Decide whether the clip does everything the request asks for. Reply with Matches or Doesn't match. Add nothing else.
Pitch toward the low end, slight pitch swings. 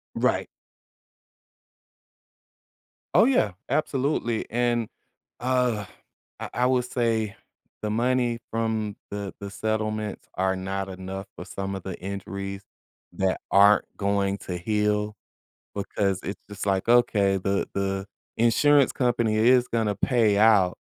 Doesn't match